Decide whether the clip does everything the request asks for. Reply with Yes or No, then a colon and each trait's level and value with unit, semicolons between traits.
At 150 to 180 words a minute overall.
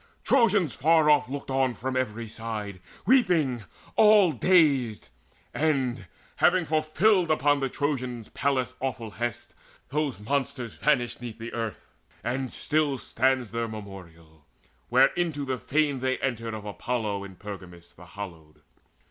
No: average, 140 wpm